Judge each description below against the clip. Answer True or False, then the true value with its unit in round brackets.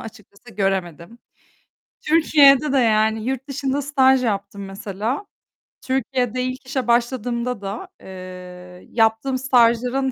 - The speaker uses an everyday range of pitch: True (4.7 semitones)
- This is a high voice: True (235 Hz)